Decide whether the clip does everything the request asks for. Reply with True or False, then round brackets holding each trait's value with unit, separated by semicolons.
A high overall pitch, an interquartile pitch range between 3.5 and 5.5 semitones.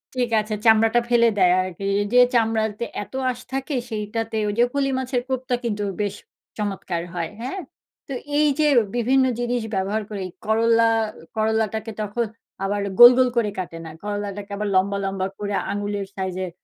False (220 Hz; 3.0 semitones)